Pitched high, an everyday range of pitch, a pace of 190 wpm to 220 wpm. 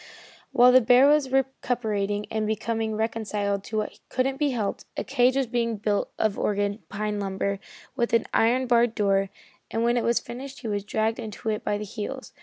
Yes: high, 225 Hz; average, 3.1 semitones; average, 195 wpm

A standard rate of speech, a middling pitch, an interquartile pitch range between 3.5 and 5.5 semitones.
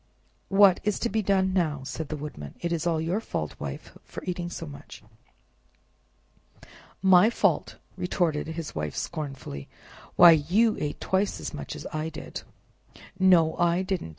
Yes: average, 150 wpm; medium, 170 Hz; average, 3.8 semitones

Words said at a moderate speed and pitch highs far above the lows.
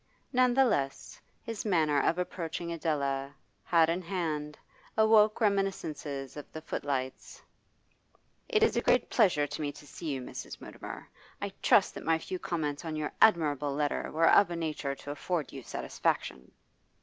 No: average, 160 wpm; average, 4.1 semitones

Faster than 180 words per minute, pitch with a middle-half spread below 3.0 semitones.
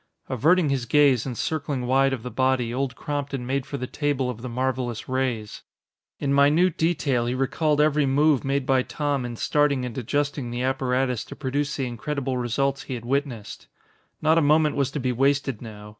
Yes: average, 190 wpm; narrow, 2.4 semitones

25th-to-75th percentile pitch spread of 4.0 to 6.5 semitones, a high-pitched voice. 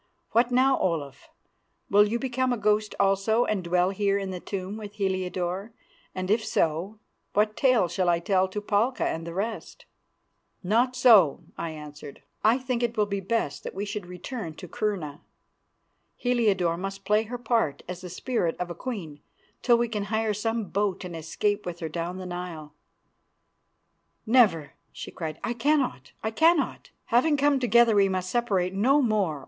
Yes: average, 4.5 semitones; high, 200 Hz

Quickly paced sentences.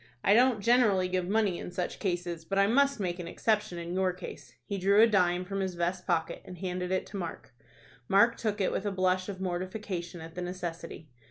Yes: fast, 220 wpm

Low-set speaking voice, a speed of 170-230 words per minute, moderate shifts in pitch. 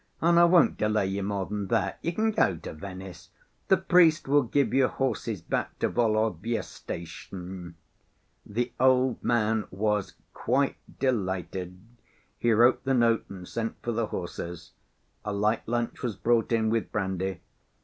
No: low, 110 Hz; average, 155 wpm; average, 4.6 semitones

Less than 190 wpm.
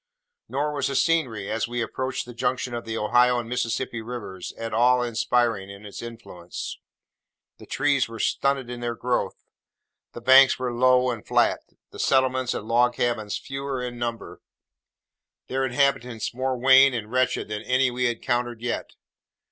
Yes: average, 165 wpm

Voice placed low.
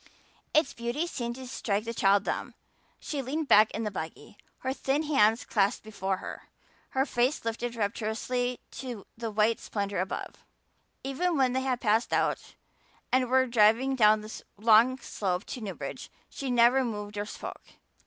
No: high, 235 Hz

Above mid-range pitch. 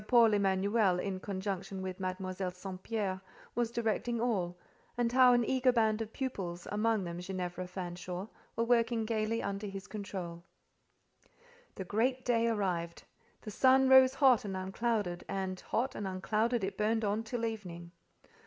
Yes: high, 205 Hz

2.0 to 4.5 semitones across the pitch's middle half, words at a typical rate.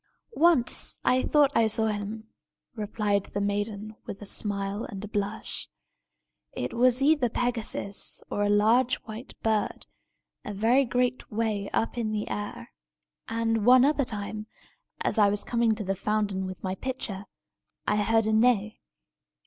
Yes: narrow, 2.5 semitones; average, 155 wpm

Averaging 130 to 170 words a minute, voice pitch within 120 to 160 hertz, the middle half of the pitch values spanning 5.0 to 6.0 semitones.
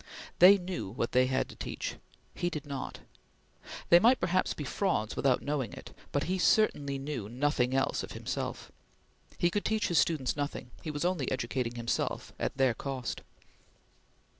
Yes: average, 165 wpm; medium, 140 Hz; average, 5.3 semitones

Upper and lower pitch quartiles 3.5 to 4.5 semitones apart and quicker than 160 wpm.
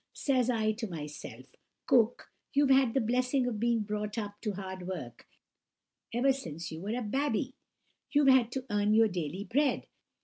Yes: average, 4.1 semitones; average, 170 wpm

